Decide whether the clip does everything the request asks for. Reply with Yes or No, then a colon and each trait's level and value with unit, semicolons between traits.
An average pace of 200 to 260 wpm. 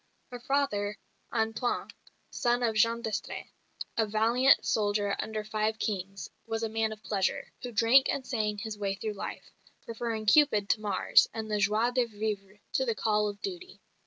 No: average, 170 wpm